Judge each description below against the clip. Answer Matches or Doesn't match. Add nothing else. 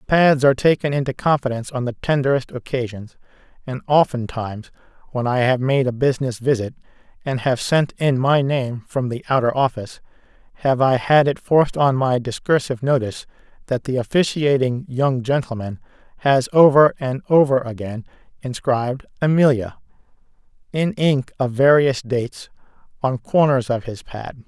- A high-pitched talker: Doesn't match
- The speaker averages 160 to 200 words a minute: Doesn't match